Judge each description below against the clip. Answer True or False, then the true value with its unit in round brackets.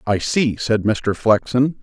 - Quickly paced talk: False (165 wpm)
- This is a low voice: True (115 Hz)